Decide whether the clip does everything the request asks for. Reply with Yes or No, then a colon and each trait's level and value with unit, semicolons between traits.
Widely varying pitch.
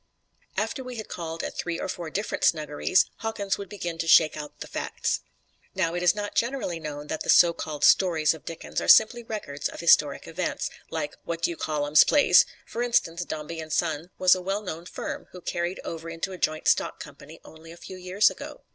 No: average, 3.2 semitones